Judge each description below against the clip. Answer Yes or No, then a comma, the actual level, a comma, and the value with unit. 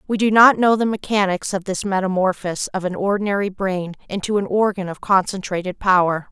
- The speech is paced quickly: No, average, 180 wpm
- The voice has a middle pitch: No, high, 195 Hz